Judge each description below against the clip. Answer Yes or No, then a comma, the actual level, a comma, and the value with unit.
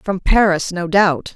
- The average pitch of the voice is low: No, medium, 185 Hz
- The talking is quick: No, average, 175 wpm